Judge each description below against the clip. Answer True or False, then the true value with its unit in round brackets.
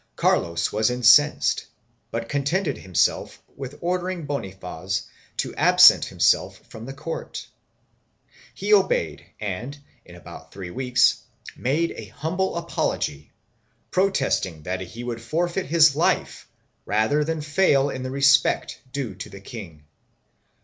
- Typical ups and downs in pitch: False (8.2 semitones)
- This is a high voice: False (135 Hz)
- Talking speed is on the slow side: True (125 wpm)